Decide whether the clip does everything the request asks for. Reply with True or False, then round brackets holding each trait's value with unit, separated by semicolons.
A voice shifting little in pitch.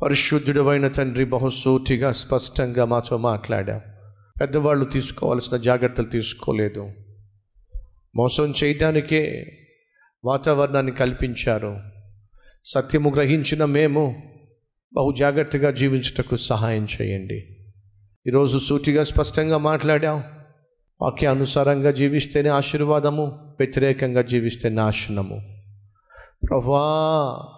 False (4.5 semitones)